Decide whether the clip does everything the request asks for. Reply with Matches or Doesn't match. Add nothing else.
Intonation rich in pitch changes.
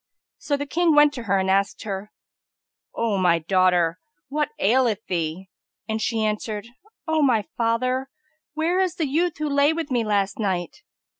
Matches